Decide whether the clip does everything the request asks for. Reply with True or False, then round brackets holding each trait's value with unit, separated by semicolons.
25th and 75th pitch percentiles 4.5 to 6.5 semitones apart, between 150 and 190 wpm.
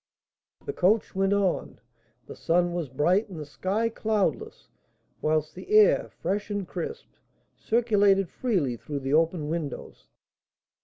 False (5.2 semitones; 135 wpm)